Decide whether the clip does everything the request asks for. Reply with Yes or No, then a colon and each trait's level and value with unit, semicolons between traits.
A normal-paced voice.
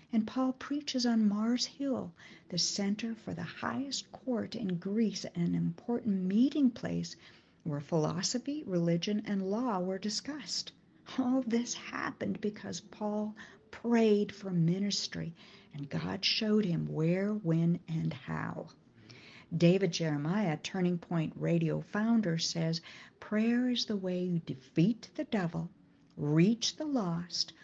No: slow, 130 wpm